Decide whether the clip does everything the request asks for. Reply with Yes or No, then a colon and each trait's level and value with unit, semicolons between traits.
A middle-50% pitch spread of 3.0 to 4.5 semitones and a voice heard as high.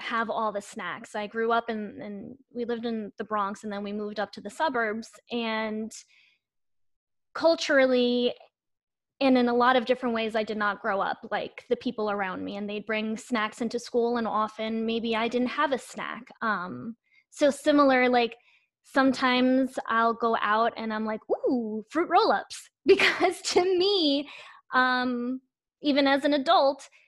Yes: average, 3.6 semitones; high, 240 Hz